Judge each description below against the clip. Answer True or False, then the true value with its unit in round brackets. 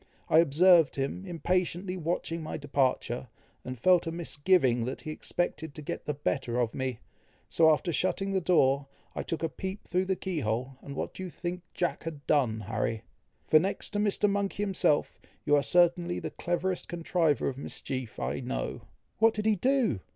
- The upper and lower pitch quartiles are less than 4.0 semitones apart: False (5.1 semitones)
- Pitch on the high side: False (165 Hz)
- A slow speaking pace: False (185 wpm)